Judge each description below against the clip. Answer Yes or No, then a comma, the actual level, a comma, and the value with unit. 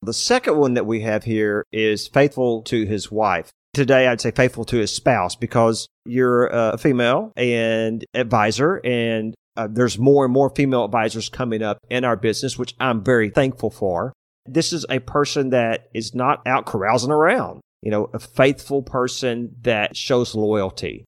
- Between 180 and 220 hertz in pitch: No, low, 120 Hz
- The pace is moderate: Yes, average, 175 wpm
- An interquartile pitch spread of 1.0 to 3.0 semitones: Yes, average, 2.7 semitones